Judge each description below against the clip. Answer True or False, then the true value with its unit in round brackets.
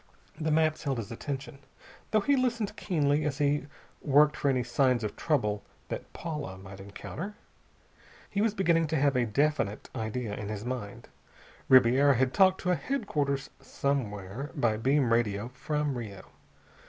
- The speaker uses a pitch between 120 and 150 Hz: True (140 Hz)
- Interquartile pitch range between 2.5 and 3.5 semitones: False (5.1 semitones)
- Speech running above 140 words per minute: True (155 wpm)